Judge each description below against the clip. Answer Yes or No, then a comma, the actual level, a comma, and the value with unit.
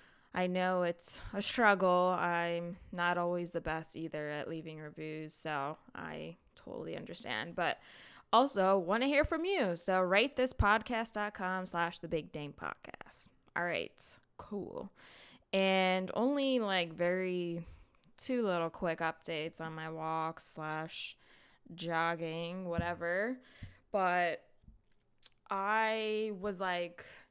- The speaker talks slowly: Yes, slow, 120 wpm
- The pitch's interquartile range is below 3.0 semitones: No, average, 3.6 semitones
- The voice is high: No, medium, 175 Hz